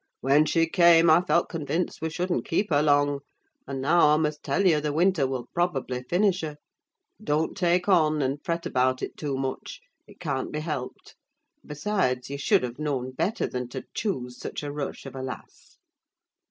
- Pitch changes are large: No, average, 4.1 semitones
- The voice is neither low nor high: Yes, medium, 150 Hz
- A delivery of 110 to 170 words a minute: No, average, 190 wpm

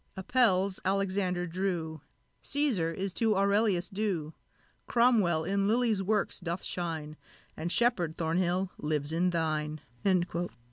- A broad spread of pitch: No, average, 3.4 semitones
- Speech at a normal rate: No, slow, 110 wpm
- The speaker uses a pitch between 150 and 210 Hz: Yes, medium, 185 Hz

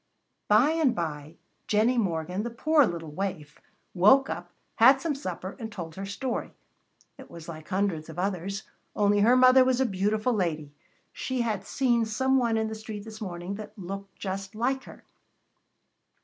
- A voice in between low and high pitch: No, high, 205 Hz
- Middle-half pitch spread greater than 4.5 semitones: Yes, average, 4.9 semitones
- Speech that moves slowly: No, average, 170 wpm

